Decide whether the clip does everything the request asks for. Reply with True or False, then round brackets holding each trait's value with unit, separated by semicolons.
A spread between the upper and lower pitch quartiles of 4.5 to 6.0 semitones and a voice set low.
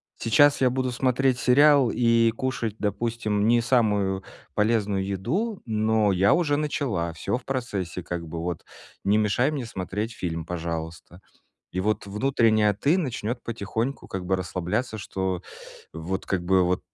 True (4.8 semitones; 105 Hz)